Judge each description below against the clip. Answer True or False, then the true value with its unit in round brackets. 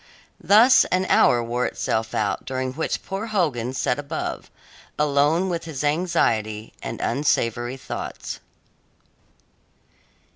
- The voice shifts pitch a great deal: True (6.0 semitones)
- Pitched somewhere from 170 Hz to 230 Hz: False (140 Hz)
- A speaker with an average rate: False (110 wpm)